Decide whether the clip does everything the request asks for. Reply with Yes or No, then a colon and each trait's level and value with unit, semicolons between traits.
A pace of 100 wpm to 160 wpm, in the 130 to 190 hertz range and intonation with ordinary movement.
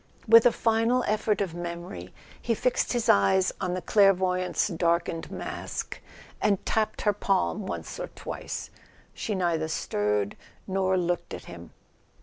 Yes: average, 140 wpm; medium, 185 Hz; average, 3.8 semitones